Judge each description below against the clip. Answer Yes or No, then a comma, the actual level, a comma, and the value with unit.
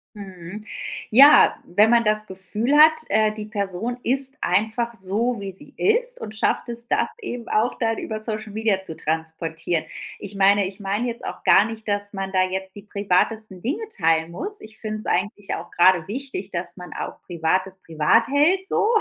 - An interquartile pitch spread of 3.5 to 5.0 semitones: Yes, average, 3.8 semitones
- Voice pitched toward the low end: No, high, 210 Hz